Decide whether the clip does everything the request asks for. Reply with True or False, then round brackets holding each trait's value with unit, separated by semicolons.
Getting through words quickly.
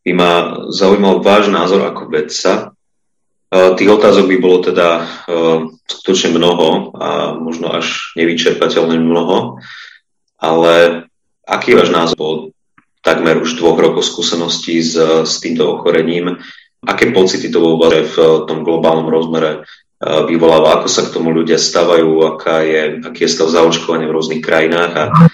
False (135 wpm)